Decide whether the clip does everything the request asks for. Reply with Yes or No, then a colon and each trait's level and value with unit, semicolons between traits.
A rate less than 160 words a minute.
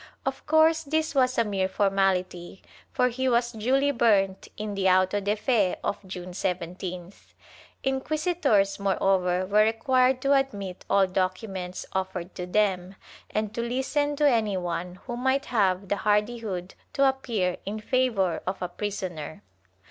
Yes: average, 150 wpm